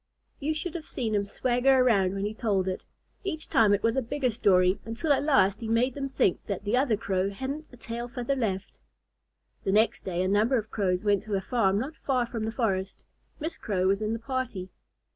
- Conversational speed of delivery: No, fast, 220 wpm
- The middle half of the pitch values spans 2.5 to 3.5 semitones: No, average, 4.7 semitones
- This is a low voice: No, high, 225 Hz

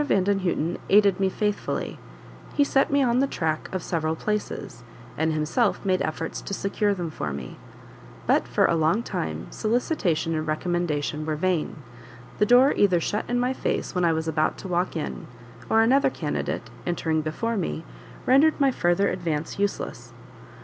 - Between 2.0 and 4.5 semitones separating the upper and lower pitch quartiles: No, average, 5.0 semitones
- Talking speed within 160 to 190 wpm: Yes, average, 165 wpm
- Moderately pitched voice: Yes, medium, 180 Hz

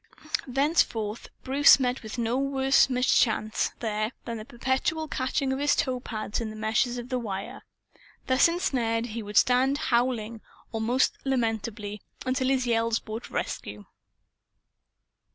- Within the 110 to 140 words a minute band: Yes, slow, 135 wpm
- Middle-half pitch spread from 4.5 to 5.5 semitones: No, average, 3.1 semitones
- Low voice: No, high, 240 Hz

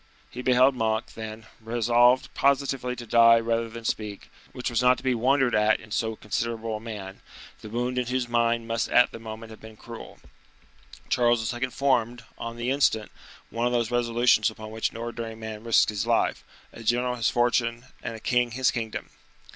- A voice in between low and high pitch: No, low, 115 Hz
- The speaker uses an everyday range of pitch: No, narrow, 1.7 semitones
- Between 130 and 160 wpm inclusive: No, average, 190 wpm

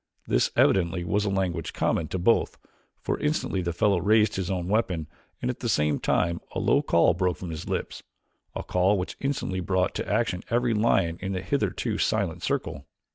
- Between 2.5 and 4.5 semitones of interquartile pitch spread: Yes, average, 3.3 semitones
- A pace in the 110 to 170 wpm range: No, average, 190 wpm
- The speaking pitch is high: No, very low, 95 Hz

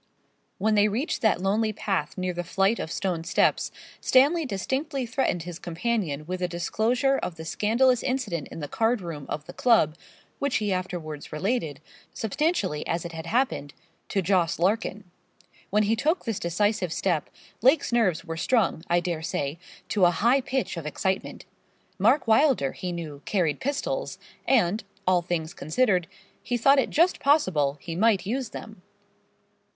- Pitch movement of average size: No, wide, 6.0 semitones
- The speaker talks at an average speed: Yes, average, 165 wpm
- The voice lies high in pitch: Yes, high, 195 Hz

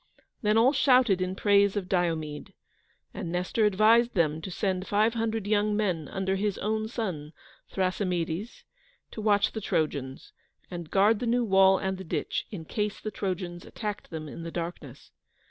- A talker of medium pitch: No, high, 195 Hz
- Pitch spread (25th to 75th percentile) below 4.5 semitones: Yes, average, 3.6 semitones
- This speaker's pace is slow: No, average, 165 wpm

